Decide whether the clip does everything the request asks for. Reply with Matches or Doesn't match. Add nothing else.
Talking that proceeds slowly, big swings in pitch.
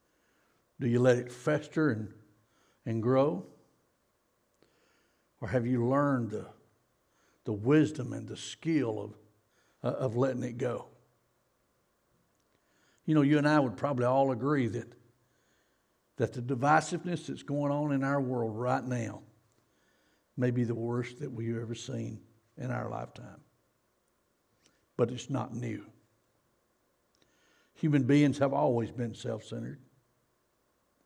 Doesn't match